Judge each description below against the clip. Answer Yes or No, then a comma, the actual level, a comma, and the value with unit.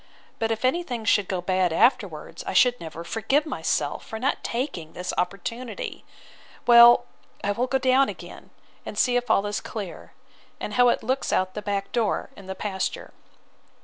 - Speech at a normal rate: Yes, average, 180 wpm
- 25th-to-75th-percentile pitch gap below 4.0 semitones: No, average, 4.6 semitones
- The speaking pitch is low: No, high, 225 Hz